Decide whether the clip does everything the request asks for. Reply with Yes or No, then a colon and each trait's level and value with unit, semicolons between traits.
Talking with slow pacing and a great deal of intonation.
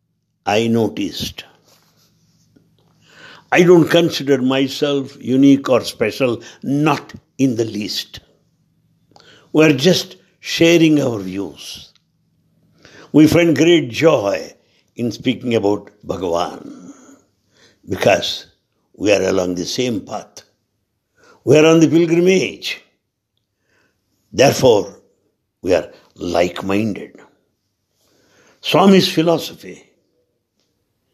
Yes: slow, 85 wpm; wide, 5.7 semitones